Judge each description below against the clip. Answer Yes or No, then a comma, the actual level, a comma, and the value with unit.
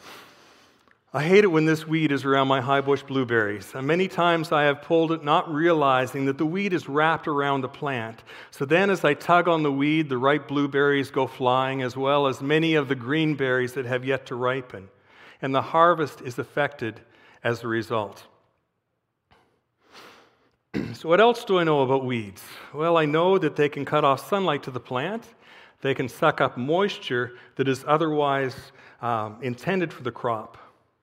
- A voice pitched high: No, medium, 140 Hz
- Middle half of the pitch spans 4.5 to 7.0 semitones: No, average, 3.4 semitones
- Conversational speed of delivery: Yes, average, 185 wpm